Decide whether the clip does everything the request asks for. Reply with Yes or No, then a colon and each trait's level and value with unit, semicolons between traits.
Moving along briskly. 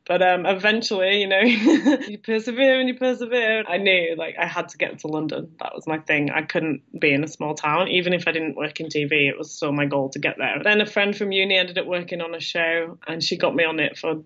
Yes: fast, 265 wpm